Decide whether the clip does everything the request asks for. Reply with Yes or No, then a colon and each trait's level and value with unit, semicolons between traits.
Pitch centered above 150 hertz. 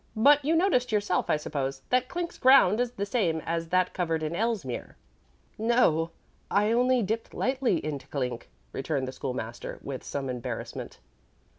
Yes: medium, 185 Hz